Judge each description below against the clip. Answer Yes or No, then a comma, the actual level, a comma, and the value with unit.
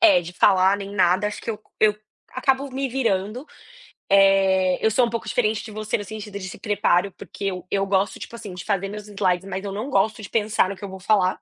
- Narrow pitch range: Yes, narrow, 2.3 semitones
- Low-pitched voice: No, high, 200 Hz